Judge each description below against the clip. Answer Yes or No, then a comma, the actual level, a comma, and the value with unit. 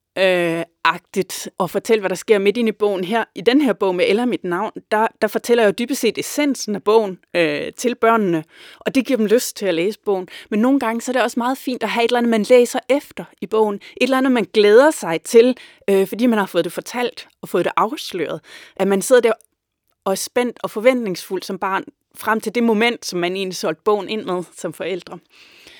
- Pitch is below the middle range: No, high, 220 Hz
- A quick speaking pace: Yes, fast, 235 wpm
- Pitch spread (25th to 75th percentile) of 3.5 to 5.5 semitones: Yes, average, 3.9 semitones